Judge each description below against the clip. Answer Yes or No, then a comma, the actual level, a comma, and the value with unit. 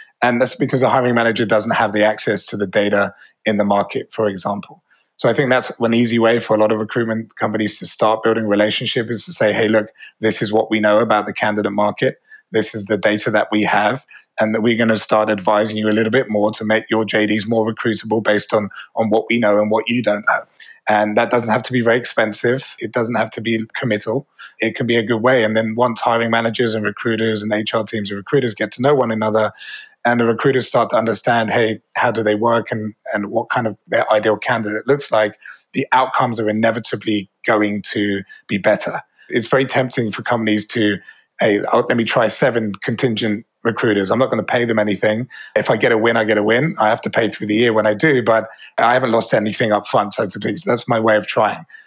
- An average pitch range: No, narrow, 1.8 semitones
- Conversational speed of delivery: No, fast, 240 wpm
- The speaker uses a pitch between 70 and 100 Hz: No, low, 110 Hz